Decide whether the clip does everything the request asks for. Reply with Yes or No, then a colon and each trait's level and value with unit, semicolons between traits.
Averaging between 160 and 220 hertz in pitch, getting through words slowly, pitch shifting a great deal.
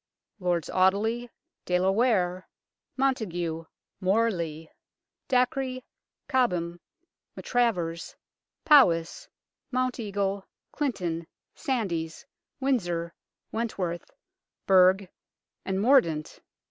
Yes: high, 190 Hz; slow, 70 wpm; wide, 6.0 semitones